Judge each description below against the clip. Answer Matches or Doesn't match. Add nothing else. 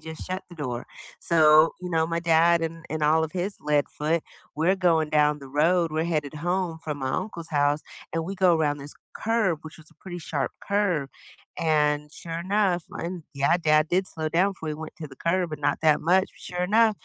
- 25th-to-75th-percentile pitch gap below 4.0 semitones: Matches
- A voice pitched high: Doesn't match